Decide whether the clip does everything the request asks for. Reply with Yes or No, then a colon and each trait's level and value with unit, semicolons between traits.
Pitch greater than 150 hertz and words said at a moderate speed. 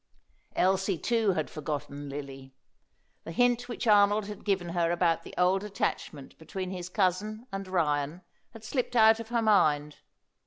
Yes: medium, 185 Hz; average, 155 wpm